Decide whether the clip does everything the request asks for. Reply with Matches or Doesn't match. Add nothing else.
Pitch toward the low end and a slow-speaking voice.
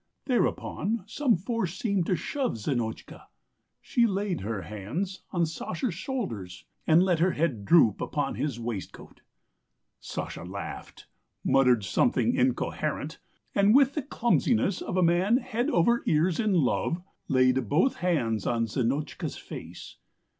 Doesn't match